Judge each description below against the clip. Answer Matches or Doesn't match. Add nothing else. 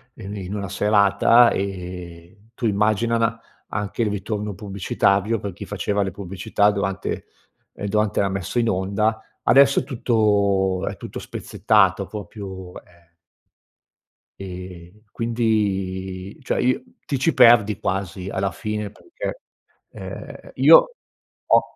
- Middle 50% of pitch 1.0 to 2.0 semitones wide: Doesn't match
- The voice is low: Matches